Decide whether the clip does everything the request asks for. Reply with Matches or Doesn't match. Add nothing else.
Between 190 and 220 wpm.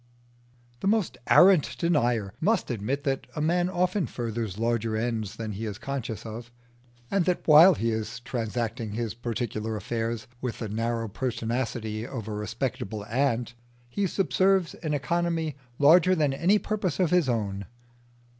Doesn't match